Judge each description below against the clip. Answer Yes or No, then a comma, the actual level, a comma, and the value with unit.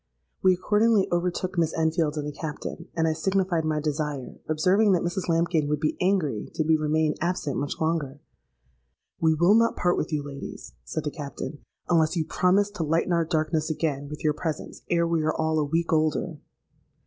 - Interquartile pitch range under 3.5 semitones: Yes, narrow, 2.4 semitones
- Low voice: No, medium, 160 Hz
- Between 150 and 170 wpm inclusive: No, average, 190 wpm